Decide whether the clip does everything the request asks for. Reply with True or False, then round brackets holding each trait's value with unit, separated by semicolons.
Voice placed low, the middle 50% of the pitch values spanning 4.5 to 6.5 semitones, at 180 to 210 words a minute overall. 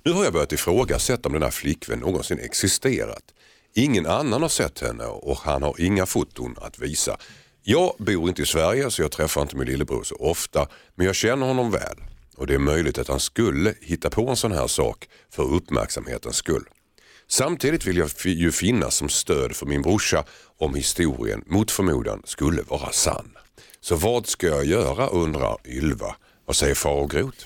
True (85 Hz; 5.1 semitones; 185 wpm)